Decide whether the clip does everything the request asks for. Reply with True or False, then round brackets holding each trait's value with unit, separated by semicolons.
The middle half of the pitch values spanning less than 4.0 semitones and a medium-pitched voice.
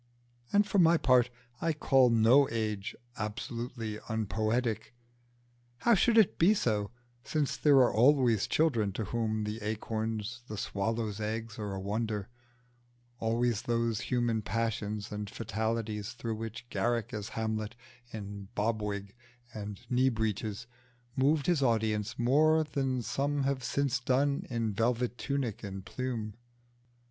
False (3.1 semitones; 115 Hz)